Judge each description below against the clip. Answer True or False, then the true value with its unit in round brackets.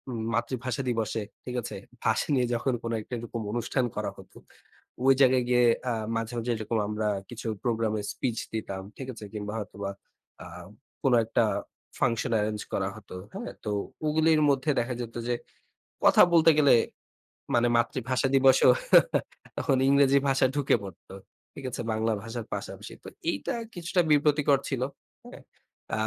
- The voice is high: False (120 Hz)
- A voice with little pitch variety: False (3.4 semitones)